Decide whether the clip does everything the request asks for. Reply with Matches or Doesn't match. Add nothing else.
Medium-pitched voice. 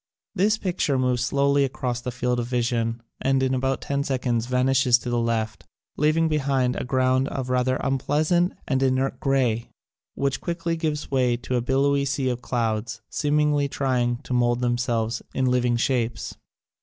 Doesn't match